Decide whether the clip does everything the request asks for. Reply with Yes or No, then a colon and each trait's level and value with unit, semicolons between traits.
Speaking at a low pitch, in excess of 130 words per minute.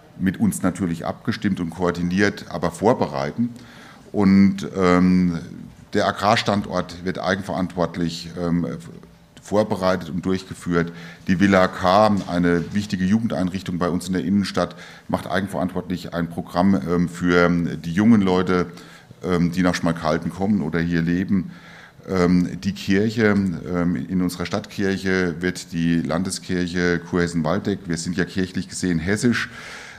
No: very low, 90 Hz; slow, 125 wpm